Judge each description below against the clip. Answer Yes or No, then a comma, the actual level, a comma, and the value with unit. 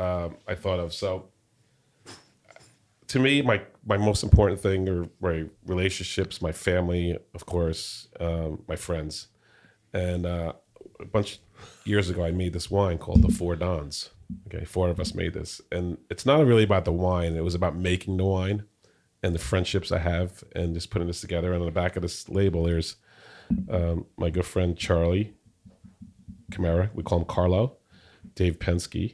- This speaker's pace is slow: No, average, 175 wpm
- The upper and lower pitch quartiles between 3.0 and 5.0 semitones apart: No, narrow, 2.5 semitones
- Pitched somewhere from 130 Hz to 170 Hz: No, very low, 90 Hz